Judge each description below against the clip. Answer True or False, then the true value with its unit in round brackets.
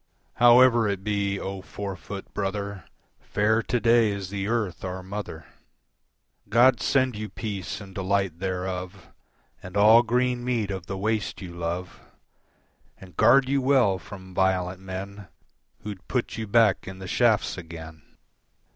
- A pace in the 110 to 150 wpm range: True (145 wpm)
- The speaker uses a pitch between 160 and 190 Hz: False (100 Hz)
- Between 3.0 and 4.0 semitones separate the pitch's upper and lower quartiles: True (3.3 semitones)